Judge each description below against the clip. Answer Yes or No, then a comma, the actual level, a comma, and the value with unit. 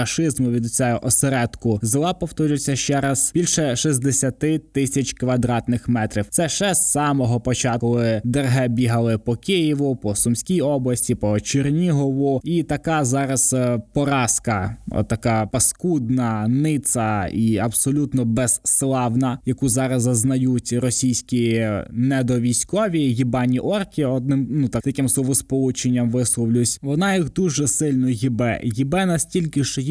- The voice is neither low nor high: No, low, 130 Hz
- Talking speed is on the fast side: No, average, 120 wpm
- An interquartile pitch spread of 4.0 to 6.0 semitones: No, average, 2.9 semitones